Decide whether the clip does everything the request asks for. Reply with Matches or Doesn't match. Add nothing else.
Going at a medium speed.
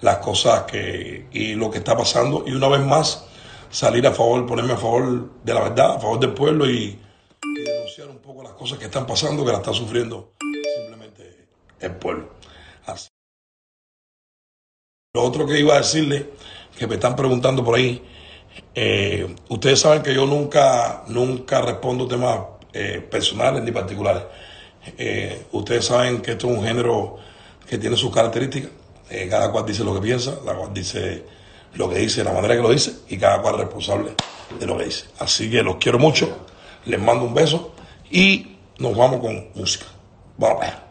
Matches